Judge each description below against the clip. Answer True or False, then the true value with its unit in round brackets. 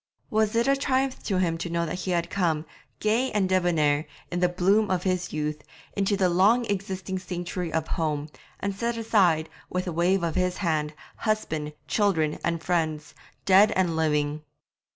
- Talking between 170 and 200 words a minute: True (175 wpm)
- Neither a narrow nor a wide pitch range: True (3.7 semitones)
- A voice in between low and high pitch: True (180 Hz)